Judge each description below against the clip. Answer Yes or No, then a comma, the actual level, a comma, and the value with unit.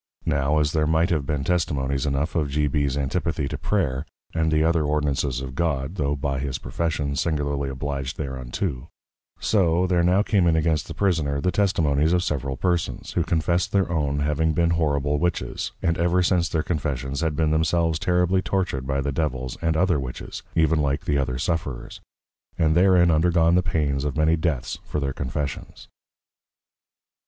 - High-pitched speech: No, very low, 75 Hz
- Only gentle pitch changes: No, average, 3.2 semitones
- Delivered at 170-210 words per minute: Yes, average, 175 wpm